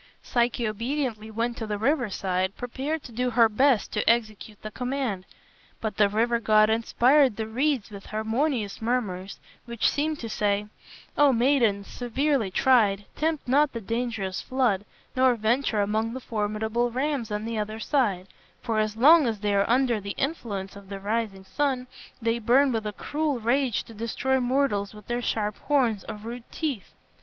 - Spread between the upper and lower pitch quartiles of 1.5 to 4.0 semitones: Yes, average, 3.6 semitones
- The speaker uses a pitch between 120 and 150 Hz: No, high, 230 Hz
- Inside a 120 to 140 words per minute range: No, average, 170 wpm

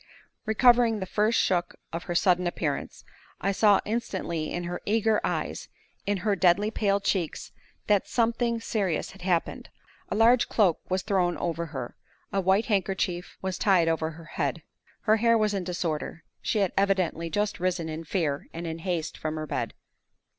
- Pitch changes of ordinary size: Yes, average, 3.7 semitones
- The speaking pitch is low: No, high, 190 Hz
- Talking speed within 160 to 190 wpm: Yes, average, 170 wpm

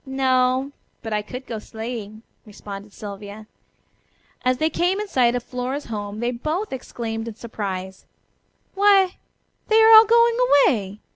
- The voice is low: No, high, 245 Hz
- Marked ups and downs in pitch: Yes, wide, 6.8 semitones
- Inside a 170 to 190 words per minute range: No, average, 145 wpm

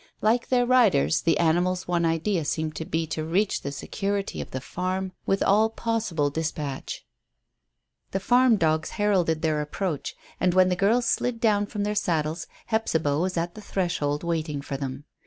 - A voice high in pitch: No, medium, 175 Hz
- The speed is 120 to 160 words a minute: No, average, 175 wpm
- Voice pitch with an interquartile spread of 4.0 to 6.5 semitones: Yes, average, 4.7 semitones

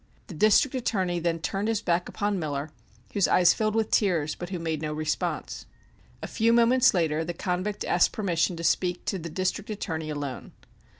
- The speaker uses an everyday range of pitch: Yes, average, 4.3 semitones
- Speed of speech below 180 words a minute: No, average, 185 wpm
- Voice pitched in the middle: Yes, medium, 180 Hz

